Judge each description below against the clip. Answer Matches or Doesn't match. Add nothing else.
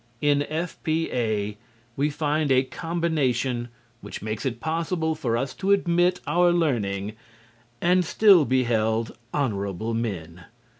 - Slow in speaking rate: Matches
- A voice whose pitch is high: Doesn't match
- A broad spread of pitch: Matches